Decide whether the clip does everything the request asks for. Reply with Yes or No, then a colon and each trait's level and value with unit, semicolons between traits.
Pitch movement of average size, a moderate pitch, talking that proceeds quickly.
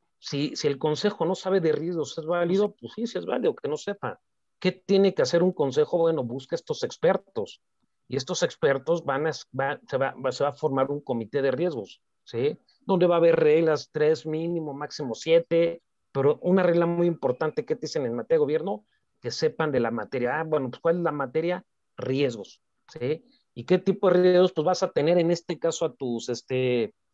Yes: average, 3.9 semitones; medium, 170 Hz; fast, 210 wpm